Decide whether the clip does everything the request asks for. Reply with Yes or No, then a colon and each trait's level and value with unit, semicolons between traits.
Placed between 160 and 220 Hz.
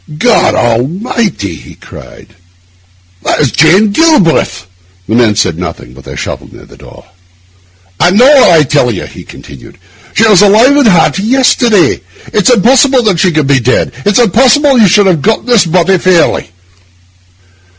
Yes: high, 190 Hz